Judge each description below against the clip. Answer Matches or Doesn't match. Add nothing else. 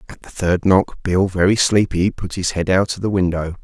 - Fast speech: Matches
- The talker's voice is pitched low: Matches